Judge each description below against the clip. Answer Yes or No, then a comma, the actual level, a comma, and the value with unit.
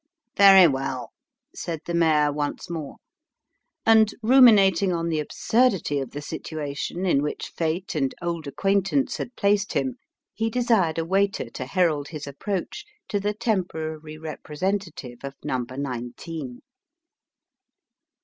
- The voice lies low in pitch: No, medium, 165 Hz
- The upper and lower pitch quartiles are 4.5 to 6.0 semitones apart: Yes, wide, 5.4 semitones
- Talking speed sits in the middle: No, slow, 130 wpm